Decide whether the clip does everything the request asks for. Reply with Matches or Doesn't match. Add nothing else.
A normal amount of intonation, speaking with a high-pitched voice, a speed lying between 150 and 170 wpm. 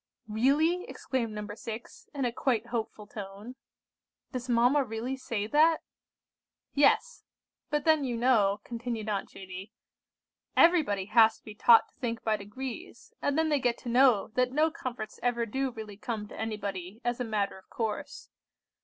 Matches